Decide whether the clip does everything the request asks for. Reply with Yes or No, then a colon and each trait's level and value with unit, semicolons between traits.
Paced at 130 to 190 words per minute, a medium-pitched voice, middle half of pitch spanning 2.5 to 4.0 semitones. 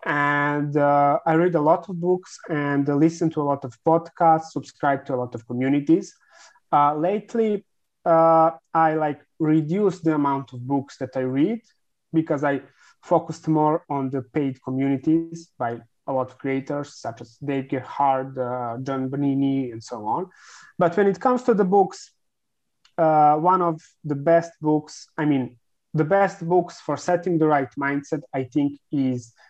Yes: average, 170 wpm; medium, 150 Hz; average, 3.7 semitones